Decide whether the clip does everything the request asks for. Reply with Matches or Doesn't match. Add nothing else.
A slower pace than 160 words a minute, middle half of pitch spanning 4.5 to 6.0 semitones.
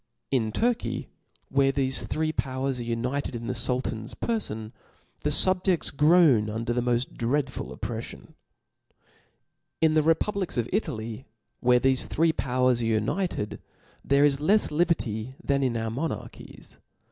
Matches